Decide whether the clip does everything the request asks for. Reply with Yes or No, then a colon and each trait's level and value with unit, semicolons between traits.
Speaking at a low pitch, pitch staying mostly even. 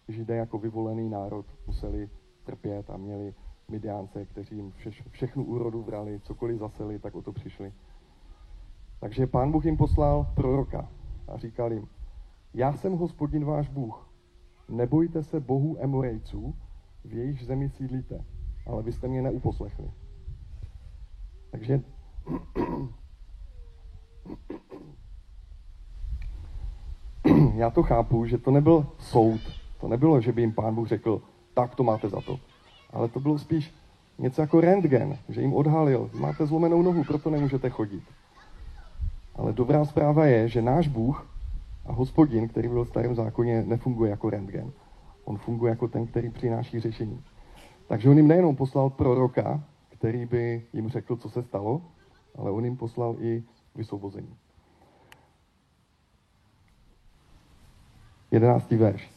No: low, 115 Hz; average, 4.7 semitones